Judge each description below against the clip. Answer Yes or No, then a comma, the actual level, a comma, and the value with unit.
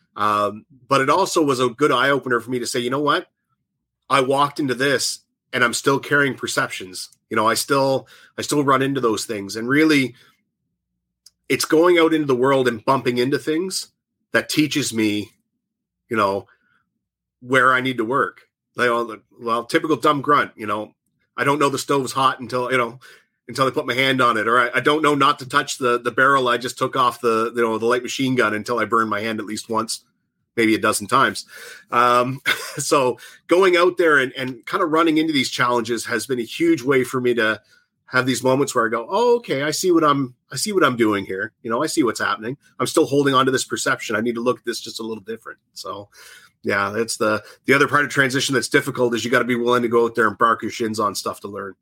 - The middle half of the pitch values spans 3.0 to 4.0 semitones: Yes, average, 3.6 semitones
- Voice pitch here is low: Yes, low, 130 Hz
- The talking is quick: Yes, fast, 235 wpm